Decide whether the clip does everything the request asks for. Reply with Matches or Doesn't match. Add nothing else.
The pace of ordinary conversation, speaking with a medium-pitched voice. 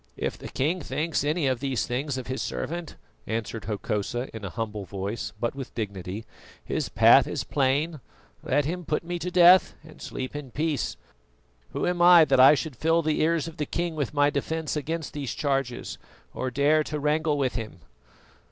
Matches